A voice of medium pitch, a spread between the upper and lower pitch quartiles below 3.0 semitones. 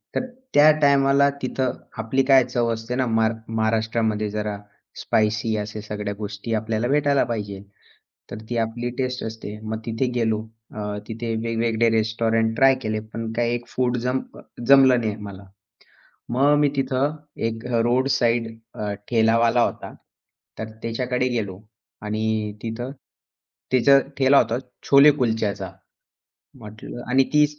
No: low, 115 Hz; narrow, 2.6 semitones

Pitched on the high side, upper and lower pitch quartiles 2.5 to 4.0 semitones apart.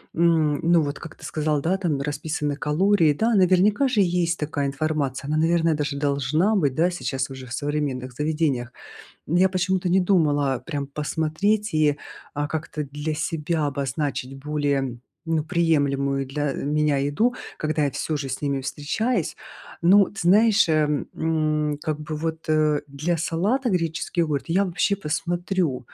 No: medium, 155 Hz; average, 3.3 semitones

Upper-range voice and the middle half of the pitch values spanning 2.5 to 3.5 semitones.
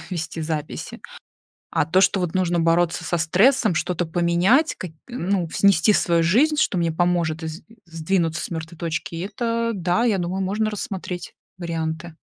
No: medium, 175 Hz; average, 3.0 semitones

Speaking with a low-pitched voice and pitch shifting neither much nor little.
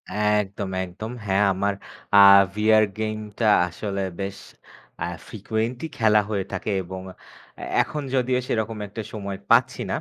No: low, 105 Hz; narrow, 1.9 semitones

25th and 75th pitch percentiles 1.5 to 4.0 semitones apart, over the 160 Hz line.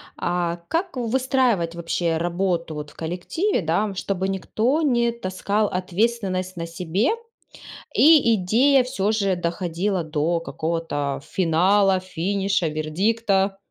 No: average, 4.5 semitones; medium, 185 Hz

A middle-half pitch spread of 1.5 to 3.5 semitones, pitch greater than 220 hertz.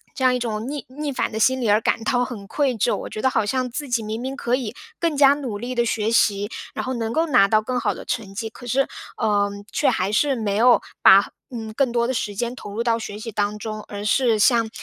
Yes: average, 3.2 semitones; high, 230 Hz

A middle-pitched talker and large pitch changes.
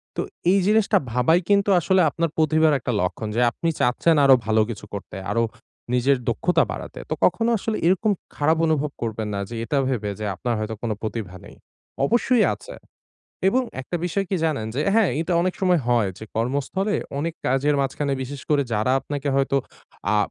Yes: medium, 145 Hz; wide, 7.1 semitones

